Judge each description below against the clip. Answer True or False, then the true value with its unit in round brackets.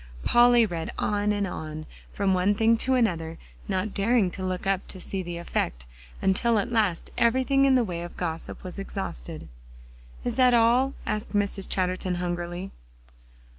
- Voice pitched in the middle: False (195 Hz)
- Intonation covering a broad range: False (4.5 semitones)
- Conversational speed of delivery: True (165 wpm)